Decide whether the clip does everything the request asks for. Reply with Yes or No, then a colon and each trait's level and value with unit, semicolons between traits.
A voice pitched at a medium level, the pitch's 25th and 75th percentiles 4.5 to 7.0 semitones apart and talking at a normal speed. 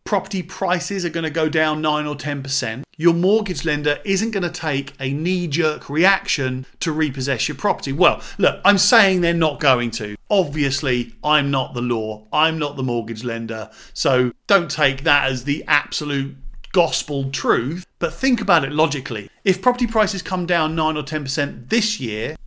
Yes: medium, 150 Hz; average, 4.9 semitones; average, 180 wpm